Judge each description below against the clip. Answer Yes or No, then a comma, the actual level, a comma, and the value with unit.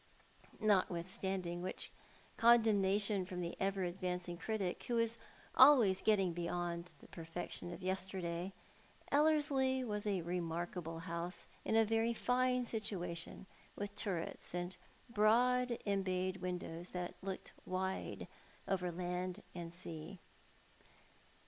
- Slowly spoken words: Yes, slow, 110 wpm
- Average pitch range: Yes, average, 3.7 semitones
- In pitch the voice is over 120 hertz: Yes, medium, 185 Hz